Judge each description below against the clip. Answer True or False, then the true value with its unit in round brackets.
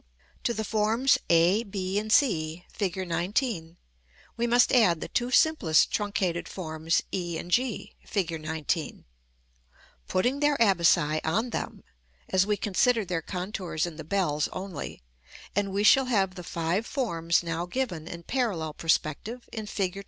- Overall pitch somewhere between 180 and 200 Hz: True (185 Hz)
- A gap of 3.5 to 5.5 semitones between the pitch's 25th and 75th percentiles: True (4.9 semitones)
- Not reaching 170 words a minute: True (150 wpm)